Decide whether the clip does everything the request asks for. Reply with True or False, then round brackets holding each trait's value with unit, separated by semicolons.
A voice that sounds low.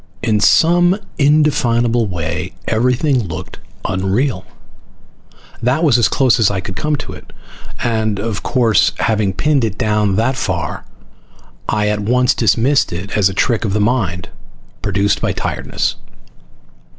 True (110 Hz)